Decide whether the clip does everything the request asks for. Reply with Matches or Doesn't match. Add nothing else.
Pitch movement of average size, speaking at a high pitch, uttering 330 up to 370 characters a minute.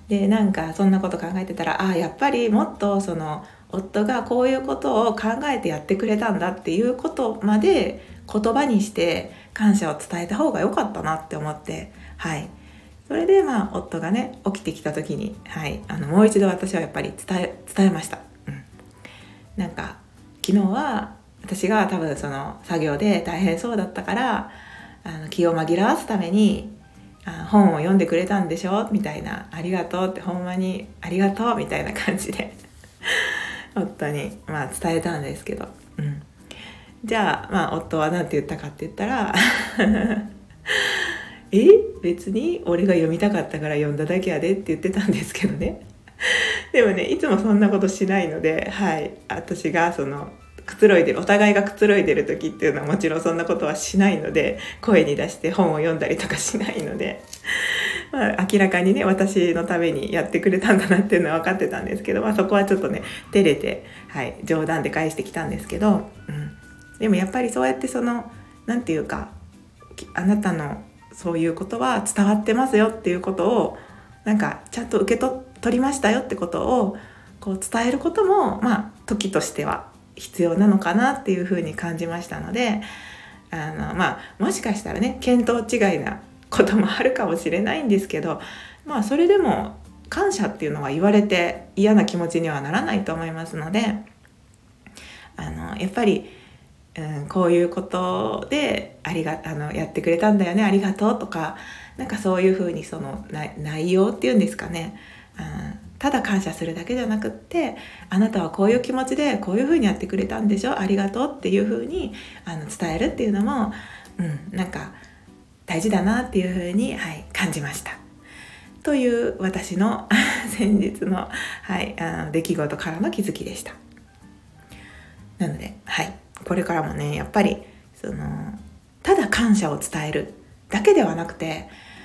Matches